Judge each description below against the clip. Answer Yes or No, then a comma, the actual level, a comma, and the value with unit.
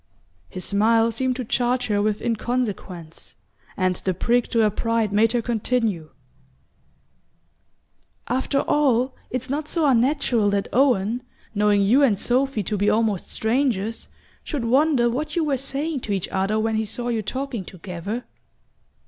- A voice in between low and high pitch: No, high, 230 Hz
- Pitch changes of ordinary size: Yes, average, 3.9 semitones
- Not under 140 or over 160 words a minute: Yes, average, 150 wpm